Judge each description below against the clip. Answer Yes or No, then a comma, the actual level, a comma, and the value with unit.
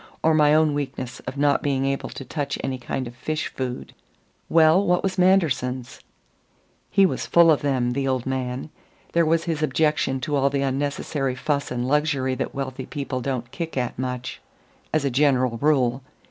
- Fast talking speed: No, average, 180 wpm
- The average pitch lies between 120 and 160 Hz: Yes, medium, 140 Hz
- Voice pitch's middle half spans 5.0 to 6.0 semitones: No, average, 3.0 semitones